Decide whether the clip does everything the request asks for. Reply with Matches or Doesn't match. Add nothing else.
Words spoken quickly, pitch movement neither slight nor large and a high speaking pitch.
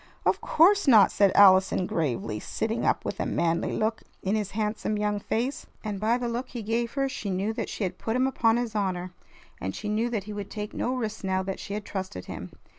Matches